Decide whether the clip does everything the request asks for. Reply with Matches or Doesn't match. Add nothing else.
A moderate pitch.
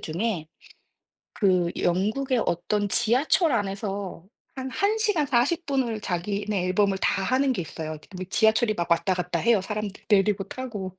Doesn't match